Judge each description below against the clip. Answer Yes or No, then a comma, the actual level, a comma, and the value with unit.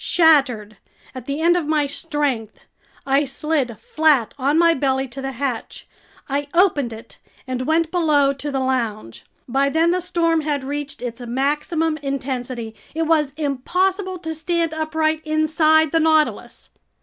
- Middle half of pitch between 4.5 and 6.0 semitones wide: No, average, 3.4 semitones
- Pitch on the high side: Yes, very high, 290 Hz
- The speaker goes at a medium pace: Yes, average, 150 wpm